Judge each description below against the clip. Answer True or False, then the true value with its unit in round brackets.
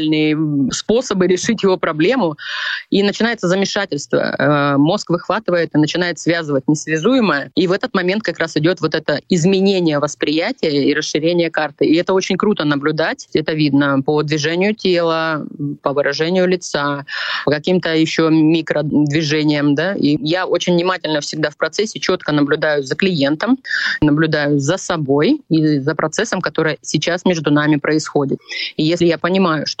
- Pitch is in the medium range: True (160 Hz)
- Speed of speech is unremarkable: True (145 wpm)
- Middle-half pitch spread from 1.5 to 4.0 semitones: True (3.4 semitones)